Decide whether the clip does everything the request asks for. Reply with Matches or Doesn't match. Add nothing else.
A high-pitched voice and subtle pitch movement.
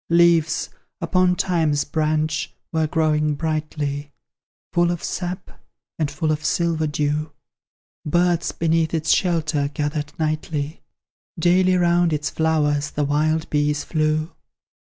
Doesn't match